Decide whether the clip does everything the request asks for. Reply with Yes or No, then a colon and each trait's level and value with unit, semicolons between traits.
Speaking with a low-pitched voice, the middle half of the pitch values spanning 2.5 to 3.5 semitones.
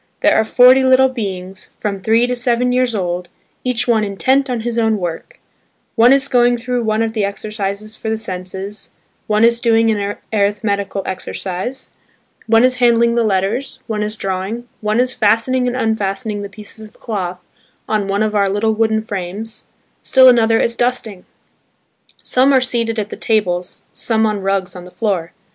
No: high, 220 Hz; average, 3.1 semitones